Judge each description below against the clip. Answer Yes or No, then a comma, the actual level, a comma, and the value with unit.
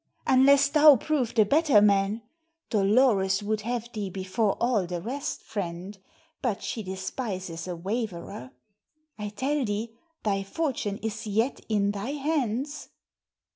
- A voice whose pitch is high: Yes, high, 215 Hz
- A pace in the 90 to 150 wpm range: Yes, slow, 135 wpm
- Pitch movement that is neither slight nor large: Yes, average, 4.7 semitones